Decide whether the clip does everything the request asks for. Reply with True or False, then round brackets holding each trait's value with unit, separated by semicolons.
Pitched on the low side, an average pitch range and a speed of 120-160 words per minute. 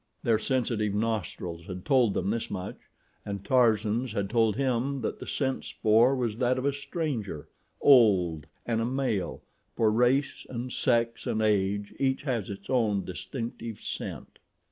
True (115 Hz; 3.8 semitones; 150 wpm)